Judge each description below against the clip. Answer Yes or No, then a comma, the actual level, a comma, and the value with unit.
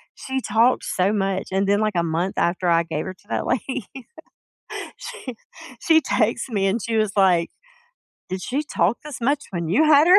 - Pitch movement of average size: No, wide, 5.7 semitones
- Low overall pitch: No, high, 205 Hz